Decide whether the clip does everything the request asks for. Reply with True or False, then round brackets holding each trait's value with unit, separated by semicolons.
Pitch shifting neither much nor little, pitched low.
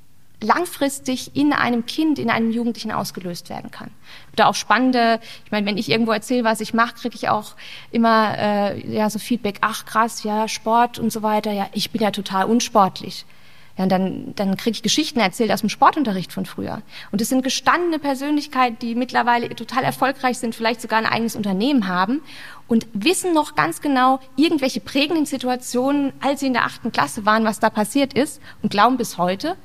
False (3.7 semitones; 230 Hz)